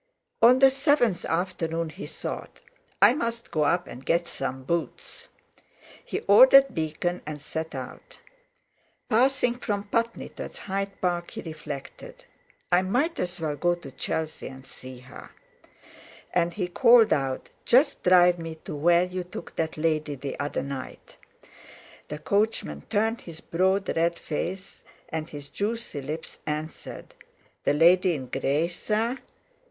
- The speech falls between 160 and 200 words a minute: No, average, 145 wpm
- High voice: No, medium, 175 Hz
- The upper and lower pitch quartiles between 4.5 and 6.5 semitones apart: Yes, average, 5.1 semitones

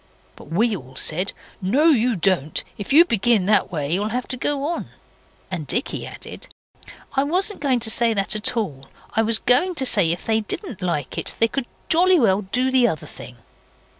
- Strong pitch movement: Yes, wide, 6.0 semitones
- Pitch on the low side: No, high, 225 Hz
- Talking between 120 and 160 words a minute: No, average, 195 wpm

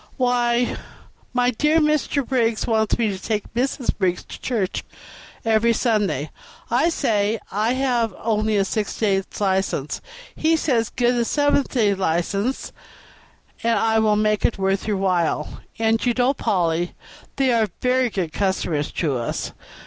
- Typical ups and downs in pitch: Yes, average, 4.1 semitones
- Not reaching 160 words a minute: Yes, average, 150 wpm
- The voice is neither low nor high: No, high, 220 Hz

